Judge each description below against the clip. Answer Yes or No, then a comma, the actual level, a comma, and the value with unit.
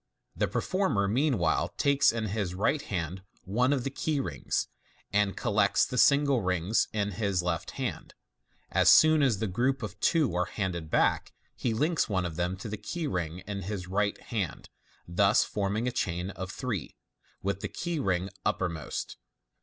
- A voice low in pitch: Yes, low, 100 Hz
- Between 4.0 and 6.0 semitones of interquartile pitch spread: Yes, wide, 5.6 semitones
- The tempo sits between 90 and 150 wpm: No, average, 170 wpm